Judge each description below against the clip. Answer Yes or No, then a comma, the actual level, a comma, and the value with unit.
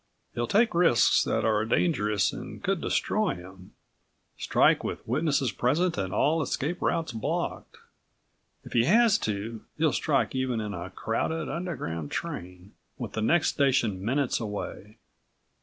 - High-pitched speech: No, low, 120 Hz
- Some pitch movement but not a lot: No, wide, 7.4 semitones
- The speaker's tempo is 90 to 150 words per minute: Yes, average, 140 wpm